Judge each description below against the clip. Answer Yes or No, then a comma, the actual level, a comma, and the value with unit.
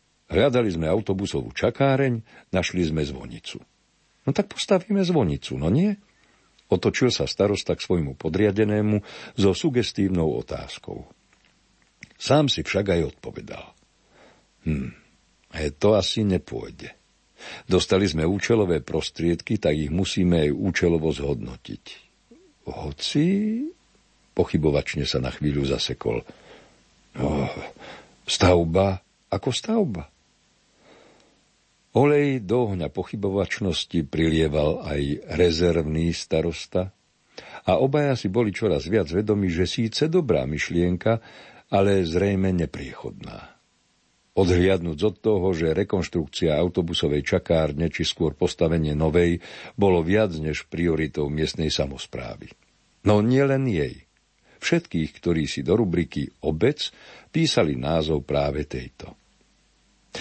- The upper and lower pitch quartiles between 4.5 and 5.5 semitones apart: Yes, average, 5.2 semitones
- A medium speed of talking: No, slow, 105 wpm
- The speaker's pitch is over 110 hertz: No, very low, 90 Hz